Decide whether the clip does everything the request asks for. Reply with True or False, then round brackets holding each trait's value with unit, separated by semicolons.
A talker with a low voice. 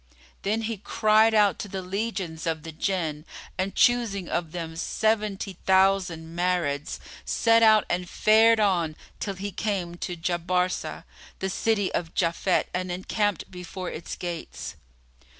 False (185 Hz)